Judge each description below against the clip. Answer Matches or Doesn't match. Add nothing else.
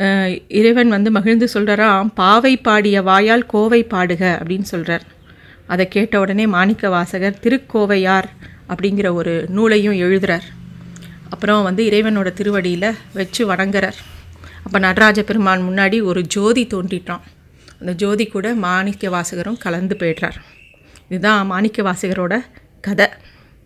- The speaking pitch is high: Matches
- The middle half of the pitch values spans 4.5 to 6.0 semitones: Doesn't match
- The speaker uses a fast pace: Doesn't match